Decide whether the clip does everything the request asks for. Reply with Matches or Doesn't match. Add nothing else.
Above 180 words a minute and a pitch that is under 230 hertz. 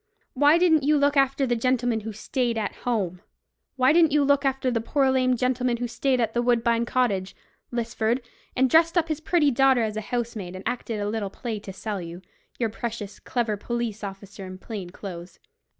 Doesn't match